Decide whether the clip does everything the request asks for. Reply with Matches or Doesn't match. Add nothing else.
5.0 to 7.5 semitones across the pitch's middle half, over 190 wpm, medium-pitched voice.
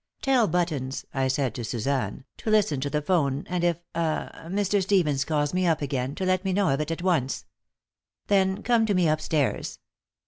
Matches